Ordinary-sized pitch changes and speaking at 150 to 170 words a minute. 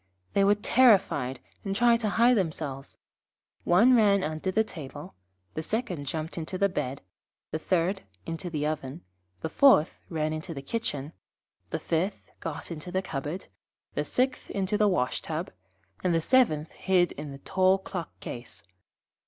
Yes: average, 4.5 semitones; average, 155 wpm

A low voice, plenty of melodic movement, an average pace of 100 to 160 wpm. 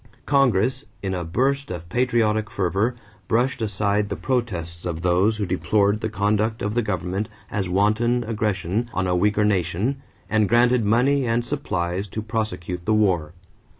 No: low, 105 Hz; average, 4.1 semitones; average, 155 wpm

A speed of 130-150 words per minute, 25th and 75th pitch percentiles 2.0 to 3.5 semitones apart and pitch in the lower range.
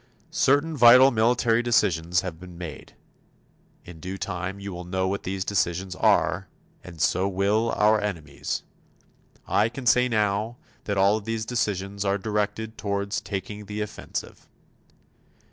Yes: average, 145 wpm; average, 2.9 semitones; low, 100 Hz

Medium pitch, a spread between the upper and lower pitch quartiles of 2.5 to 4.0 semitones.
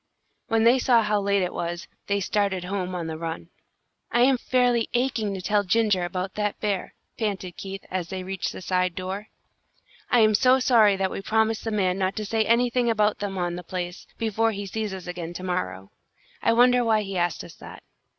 No: high, 200 Hz; average, 3.5 semitones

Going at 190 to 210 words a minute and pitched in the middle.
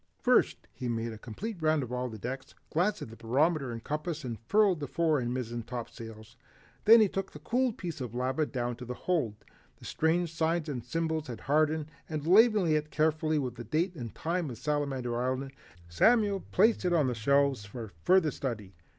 Yes: average, 195 wpm; medium, 145 Hz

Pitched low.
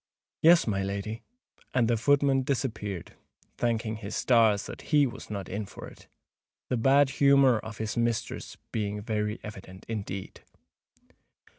Yes: low, 110 Hz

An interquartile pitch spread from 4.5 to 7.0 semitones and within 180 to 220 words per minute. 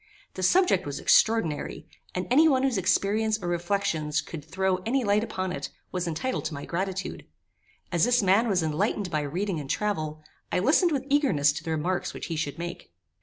Yes: average, 5.2 semitones; average, 190 wpm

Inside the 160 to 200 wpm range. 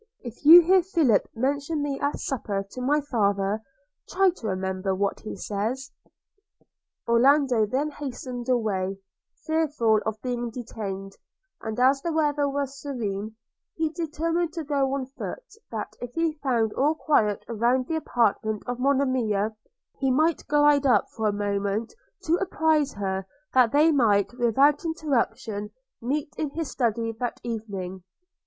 No: average, 150 wpm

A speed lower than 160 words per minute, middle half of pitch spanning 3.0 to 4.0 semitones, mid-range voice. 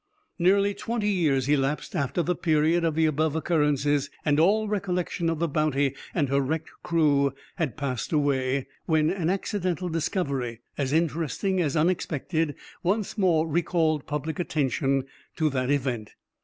Yes: average, 145 wpm; average, 3.6 semitones; medium, 155 Hz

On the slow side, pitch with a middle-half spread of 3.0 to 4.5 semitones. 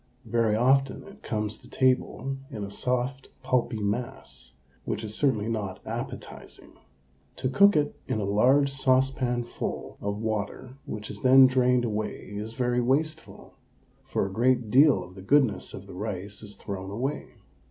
No: average, 155 wpm; average, 3.9 semitones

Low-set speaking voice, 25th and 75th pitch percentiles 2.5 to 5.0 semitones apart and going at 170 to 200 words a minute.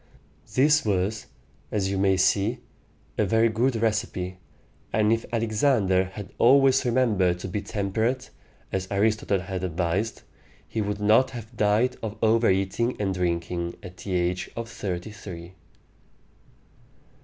No: low, 105 Hz; average, 3.5 semitones; slow, 135 wpm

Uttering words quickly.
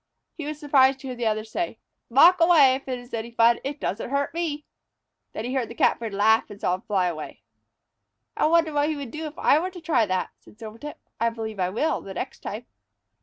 Yes: fast, 235 wpm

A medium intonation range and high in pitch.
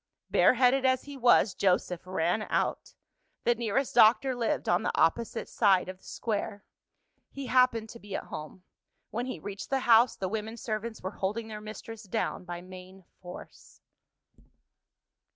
Yes: average, 4.1 semitones; high, 215 Hz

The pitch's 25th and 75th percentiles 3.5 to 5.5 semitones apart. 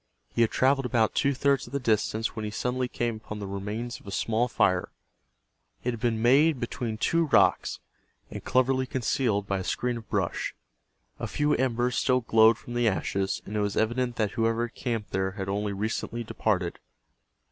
No: average, 2.9 semitones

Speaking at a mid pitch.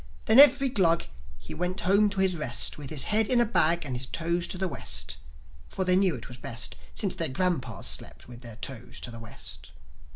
Yes: medium, 165 Hz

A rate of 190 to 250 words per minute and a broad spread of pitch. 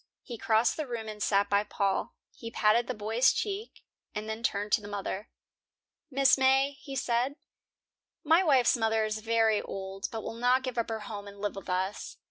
No: average, 195 wpm; average, 3.4 semitones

